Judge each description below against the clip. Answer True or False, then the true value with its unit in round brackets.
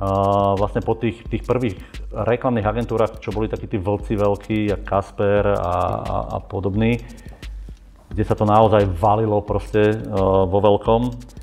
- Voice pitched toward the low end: True (105 Hz)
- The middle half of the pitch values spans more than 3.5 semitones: False (2.3 semitones)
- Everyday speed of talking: True (150 wpm)